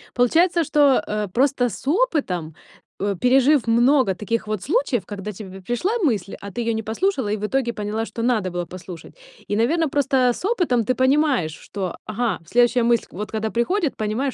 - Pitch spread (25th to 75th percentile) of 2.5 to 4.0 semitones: No, average, 4.8 semitones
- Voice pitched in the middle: No, high, 235 Hz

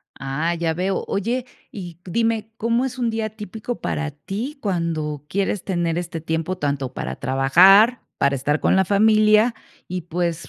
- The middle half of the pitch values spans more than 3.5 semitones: Yes, average, 5.1 semitones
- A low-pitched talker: No, medium, 185 Hz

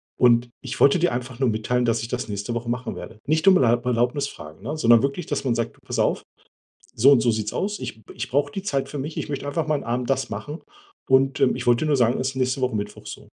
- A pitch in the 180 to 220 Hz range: No, low, 125 Hz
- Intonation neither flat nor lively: Yes, average, 3.3 semitones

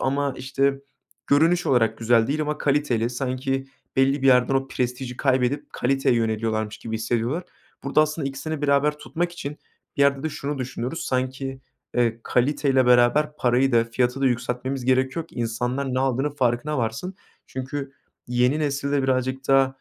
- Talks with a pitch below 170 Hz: Yes, low, 135 Hz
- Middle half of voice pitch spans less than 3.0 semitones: Yes, narrow, 2.4 semitones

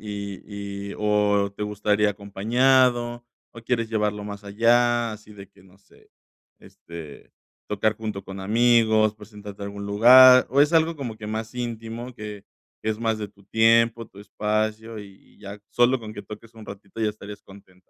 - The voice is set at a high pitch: No, low, 105 Hz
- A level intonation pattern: Yes, narrow, 2.3 semitones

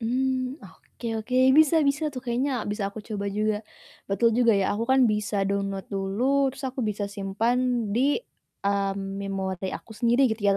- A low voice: No, high, 220 Hz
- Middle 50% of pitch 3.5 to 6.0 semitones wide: Yes, average, 4.3 semitones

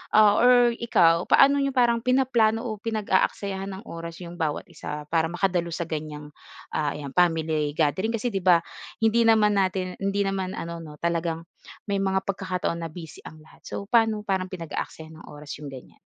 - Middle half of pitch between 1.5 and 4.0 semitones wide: No, average, 4.8 semitones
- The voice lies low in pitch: No, medium, 185 Hz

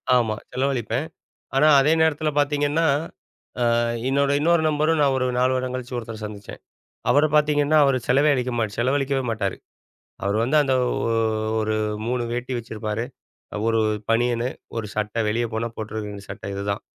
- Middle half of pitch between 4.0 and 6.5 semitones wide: Yes, average, 4.3 semitones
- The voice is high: No, low, 125 Hz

